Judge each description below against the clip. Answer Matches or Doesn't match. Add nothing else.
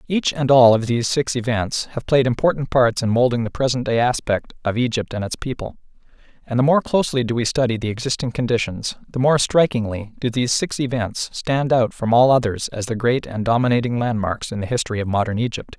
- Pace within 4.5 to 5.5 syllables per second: Doesn't match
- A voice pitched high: Doesn't match